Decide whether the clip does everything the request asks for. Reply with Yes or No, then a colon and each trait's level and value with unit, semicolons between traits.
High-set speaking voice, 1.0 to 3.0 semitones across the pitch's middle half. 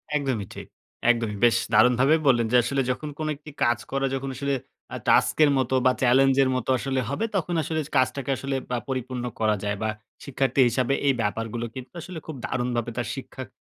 No: low, 130 Hz; narrow, 2.4 semitones